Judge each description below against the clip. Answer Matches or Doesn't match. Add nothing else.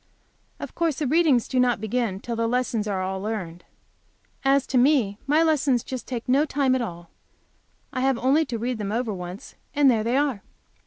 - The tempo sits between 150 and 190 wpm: Doesn't match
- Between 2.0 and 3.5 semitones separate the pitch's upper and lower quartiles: Doesn't match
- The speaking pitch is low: Doesn't match